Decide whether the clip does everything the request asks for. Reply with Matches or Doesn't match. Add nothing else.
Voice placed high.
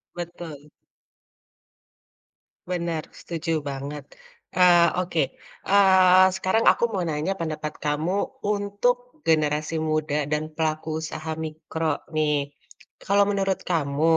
Doesn't match